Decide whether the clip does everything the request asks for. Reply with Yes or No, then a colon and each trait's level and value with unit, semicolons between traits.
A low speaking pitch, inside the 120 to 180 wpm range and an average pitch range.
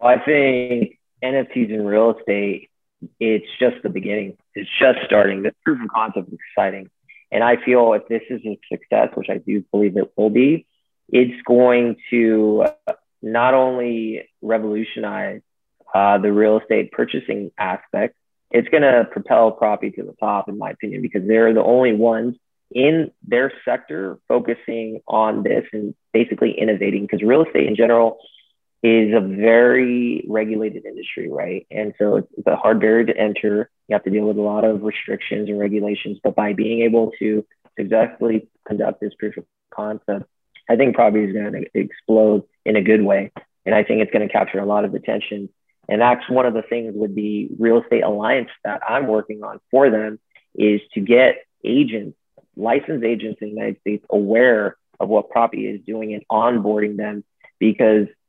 No: low, 110 Hz; average, 175 wpm; narrow, 1.9 semitones